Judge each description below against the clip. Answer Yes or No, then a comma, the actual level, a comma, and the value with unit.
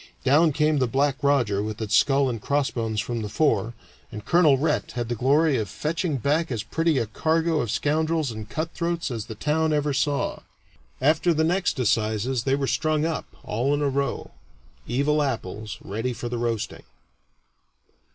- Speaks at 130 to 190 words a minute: Yes, average, 175 wpm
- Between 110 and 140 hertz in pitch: Yes, low, 135 Hz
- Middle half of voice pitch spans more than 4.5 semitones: Yes, average, 5.1 semitones